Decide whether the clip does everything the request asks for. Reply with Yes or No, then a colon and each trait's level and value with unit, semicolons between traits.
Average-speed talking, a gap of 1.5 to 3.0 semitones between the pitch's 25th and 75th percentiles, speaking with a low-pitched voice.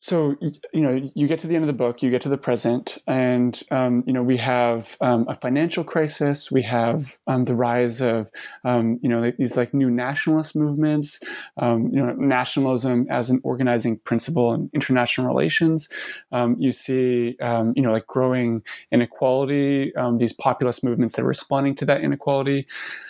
Yes: average, 180 wpm; narrow, 2.4 semitones; low, 130 Hz